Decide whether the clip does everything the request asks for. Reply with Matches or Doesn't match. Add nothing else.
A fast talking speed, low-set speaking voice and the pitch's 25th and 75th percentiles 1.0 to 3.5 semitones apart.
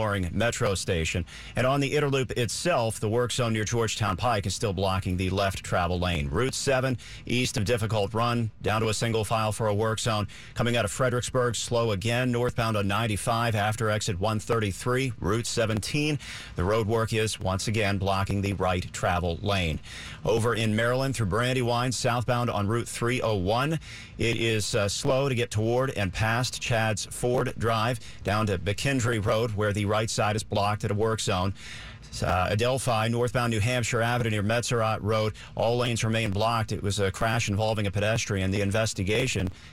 Doesn't match